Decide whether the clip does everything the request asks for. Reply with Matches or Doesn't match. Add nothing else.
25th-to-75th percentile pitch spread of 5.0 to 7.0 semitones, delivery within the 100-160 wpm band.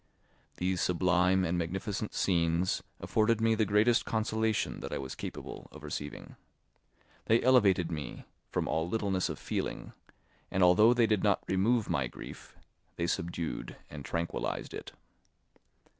Doesn't match